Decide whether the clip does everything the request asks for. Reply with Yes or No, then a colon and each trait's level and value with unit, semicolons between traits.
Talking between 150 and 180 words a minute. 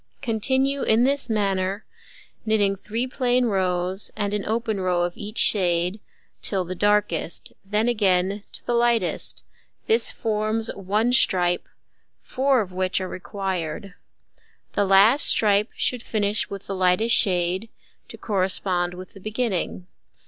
No: slow, 135 wpm